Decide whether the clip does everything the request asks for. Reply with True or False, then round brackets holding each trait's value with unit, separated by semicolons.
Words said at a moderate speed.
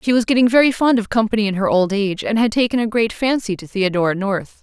False (260 wpm)